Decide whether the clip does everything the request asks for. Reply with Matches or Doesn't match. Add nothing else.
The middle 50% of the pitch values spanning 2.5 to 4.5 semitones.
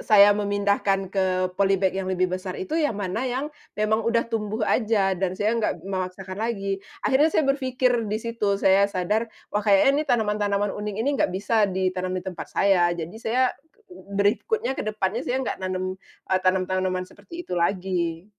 Matches